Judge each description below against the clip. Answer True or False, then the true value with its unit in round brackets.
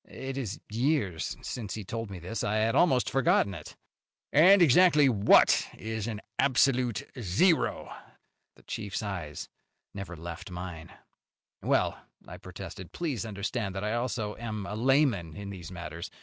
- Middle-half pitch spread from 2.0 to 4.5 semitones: False (5.3 semitones)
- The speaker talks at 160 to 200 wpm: False (150 wpm)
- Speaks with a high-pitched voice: False (110 Hz)